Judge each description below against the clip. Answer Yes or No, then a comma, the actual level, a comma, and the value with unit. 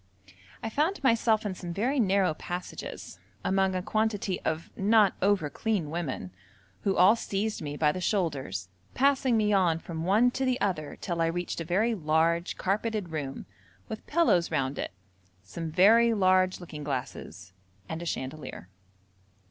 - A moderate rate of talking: Yes, average, 155 wpm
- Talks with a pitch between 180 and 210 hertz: Yes, medium, 185 Hz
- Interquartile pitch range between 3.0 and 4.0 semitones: No, average, 5.1 semitones